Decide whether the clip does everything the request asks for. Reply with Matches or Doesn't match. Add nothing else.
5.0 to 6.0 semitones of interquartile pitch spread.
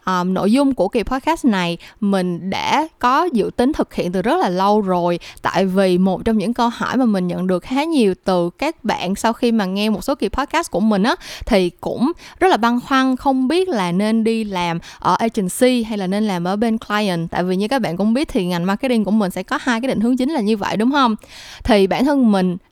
Matches